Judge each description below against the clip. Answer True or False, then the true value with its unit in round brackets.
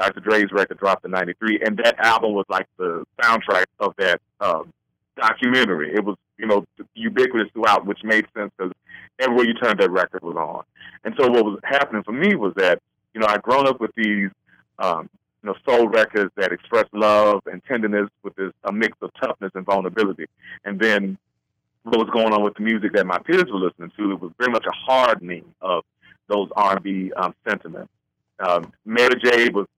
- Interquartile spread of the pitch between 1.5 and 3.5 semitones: False (4.0 semitones)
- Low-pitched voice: True (110 Hz)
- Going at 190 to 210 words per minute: True (195 wpm)